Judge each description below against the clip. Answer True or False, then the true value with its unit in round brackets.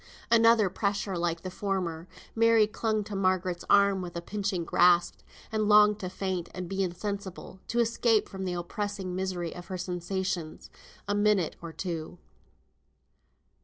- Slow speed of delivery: False (150 wpm)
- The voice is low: False (190 Hz)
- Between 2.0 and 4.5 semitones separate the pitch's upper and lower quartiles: True (2.8 semitones)